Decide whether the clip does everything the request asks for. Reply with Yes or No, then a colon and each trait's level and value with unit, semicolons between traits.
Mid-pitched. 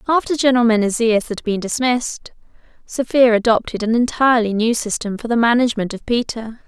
No: high, 230 Hz